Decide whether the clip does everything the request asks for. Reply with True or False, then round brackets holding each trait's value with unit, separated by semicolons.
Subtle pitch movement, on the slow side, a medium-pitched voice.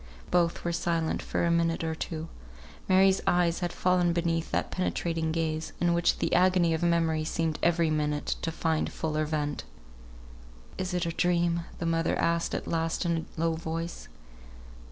False (1.2 semitones; 170 wpm; 165 Hz)